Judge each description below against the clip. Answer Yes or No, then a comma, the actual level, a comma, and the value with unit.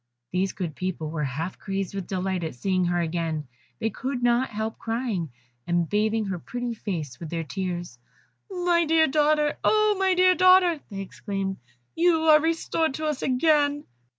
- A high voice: Yes, high, 220 Hz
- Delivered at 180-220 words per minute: No, average, 165 wpm